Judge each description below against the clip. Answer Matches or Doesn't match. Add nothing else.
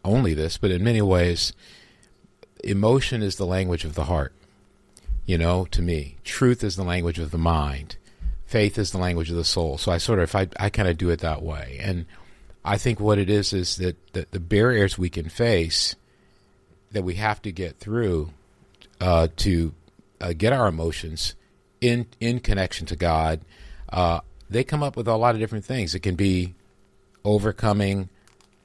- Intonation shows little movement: Doesn't match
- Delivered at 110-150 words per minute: Doesn't match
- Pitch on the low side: Matches